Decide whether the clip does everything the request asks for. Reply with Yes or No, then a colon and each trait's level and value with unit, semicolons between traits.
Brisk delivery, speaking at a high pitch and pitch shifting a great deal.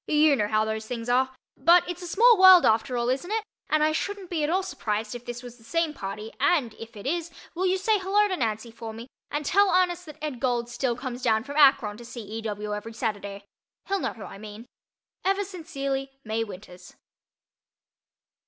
Yes: fast, 215 wpm; very high, 255 Hz; wide, 7.7 semitones